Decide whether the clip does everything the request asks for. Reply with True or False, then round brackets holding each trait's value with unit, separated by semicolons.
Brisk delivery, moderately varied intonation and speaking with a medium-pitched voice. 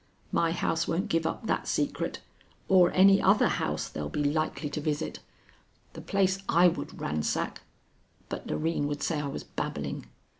False (160 wpm; 3.8 semitones; 165 Hz)